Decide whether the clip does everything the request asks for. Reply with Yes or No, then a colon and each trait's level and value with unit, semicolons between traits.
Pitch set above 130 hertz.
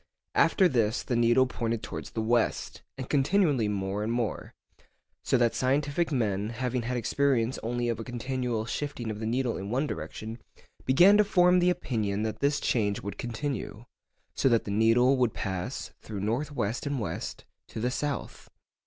No: low, 120 Hz